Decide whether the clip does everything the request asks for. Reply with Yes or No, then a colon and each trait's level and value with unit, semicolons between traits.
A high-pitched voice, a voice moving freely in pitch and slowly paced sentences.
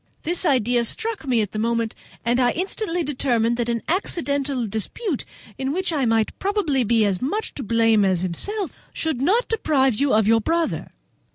No: very high, 260 Hz; wide, 6.6 semitones; average, 180 wpm